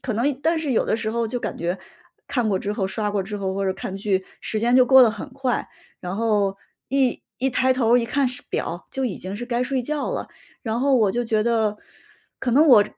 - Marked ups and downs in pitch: No, average, 3.8 semitones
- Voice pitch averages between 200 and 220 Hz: No, high, 230 Hz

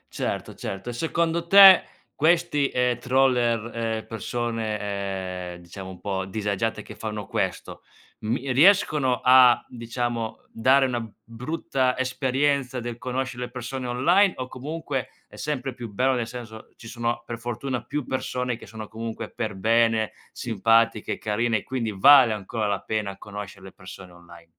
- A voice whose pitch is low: Yes, low, 120 Hz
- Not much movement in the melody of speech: No, average, 3.2 semitones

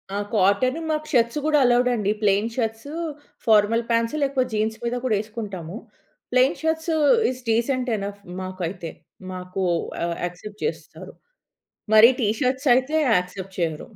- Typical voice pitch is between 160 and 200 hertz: No, high, 225 Hz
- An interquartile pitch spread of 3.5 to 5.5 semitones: Yes, average, 4.4 semitones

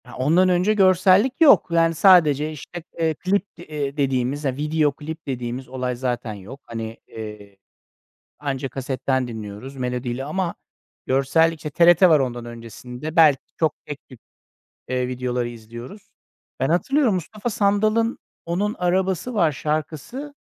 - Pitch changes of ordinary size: No, wide, 5.9 semitones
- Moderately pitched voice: Yes, medium, 150 Hz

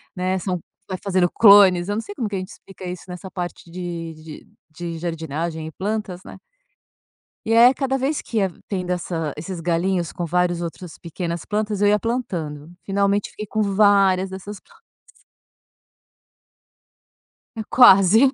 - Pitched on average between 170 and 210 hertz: Yes, medium, 185 Hz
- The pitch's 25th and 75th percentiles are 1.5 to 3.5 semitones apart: Yes, average, 3.1 semitones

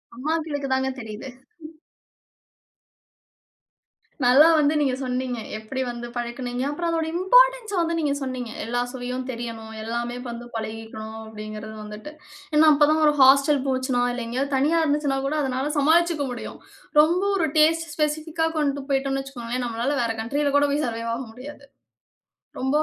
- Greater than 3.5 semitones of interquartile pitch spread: Yes, average, 4.0 semitones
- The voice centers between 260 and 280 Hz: Yes, very high, 265 Hz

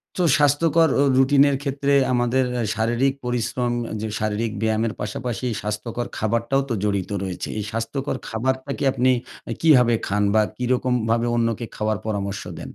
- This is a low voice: Yes, low, 120 Hz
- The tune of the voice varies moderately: Yes, average, 3.2 semitones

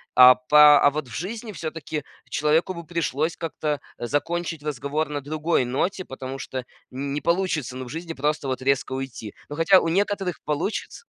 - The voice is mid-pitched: Yes, medium, 150 Hz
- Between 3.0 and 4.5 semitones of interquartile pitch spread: Yes, average, 3.9 semitones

